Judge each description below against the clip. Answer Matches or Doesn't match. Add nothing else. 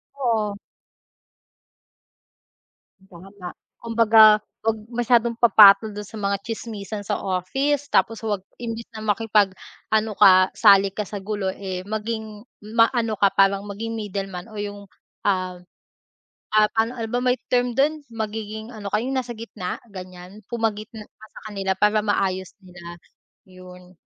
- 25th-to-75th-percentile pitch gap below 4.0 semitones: Matches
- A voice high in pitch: Matches